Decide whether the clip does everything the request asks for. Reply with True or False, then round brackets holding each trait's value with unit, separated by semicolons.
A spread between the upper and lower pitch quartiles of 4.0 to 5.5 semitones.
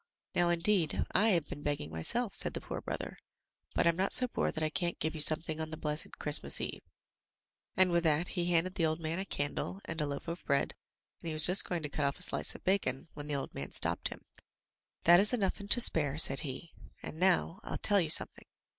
False (3.5 semitones)